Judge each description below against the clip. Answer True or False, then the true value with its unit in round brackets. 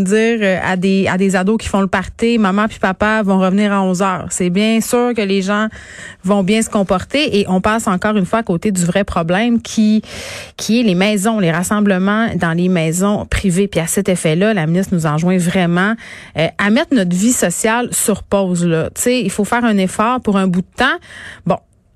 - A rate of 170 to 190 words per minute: False (210 wpm)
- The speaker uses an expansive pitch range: False (2.9 semitones)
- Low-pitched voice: False (200 Hz)